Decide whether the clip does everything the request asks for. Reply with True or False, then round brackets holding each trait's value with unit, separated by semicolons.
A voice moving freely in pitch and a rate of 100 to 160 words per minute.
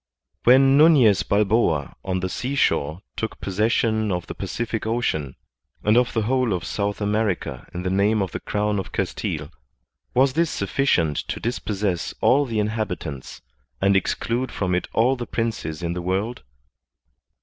False (4.3 semitones; 155 wpm)